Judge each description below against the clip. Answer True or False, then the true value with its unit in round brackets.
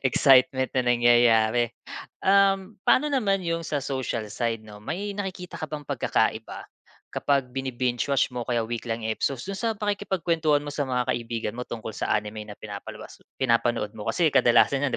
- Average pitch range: False (6.2 semitones)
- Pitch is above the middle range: False (130 Hz)